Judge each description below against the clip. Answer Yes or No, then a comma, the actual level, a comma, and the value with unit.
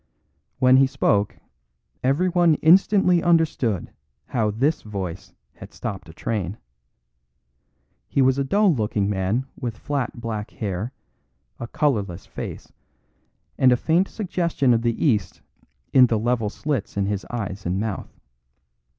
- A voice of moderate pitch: No, low, 120 Hz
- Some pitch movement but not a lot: No, wide, 5.9 semitones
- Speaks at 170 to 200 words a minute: No, slow, 135 wpm